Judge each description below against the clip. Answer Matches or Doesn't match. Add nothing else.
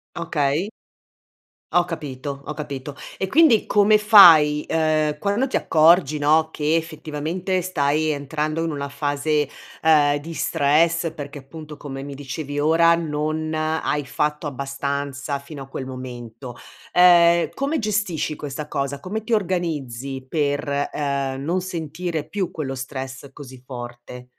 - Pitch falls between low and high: Matches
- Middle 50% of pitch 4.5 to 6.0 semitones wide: Doesn't match